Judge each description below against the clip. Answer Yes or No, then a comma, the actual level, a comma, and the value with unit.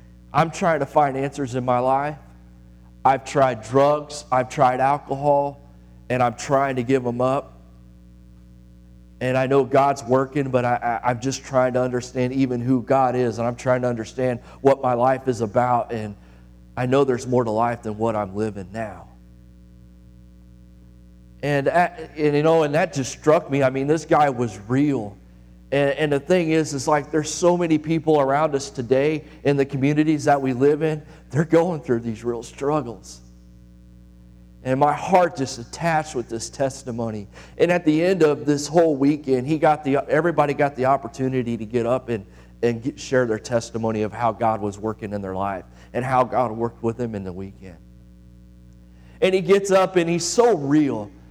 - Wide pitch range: Yes, wide, 5.8 semitones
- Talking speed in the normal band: Yes, average, 185 wpm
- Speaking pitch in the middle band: No, low, 125 Hz